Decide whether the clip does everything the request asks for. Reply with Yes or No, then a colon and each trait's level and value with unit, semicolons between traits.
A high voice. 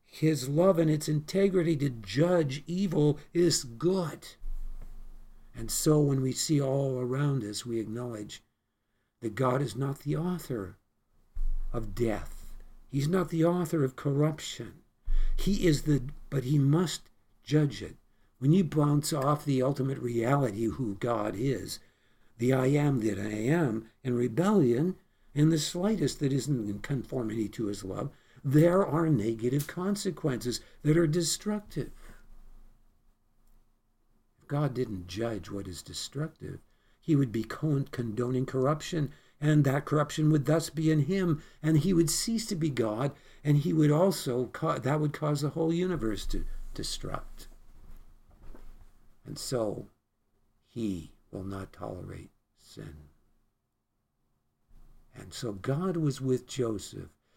No: low, 135 Hz